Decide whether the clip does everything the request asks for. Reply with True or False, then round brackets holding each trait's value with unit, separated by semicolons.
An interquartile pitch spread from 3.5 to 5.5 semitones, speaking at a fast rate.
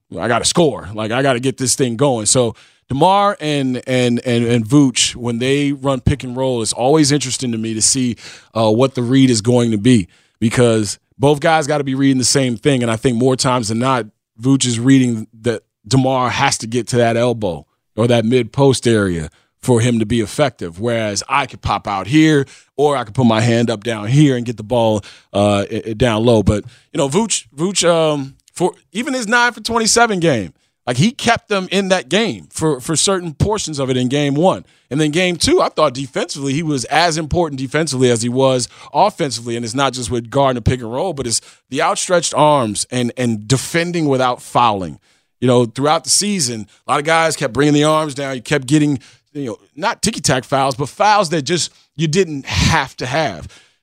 True (4.2 semitones; 220 wpm)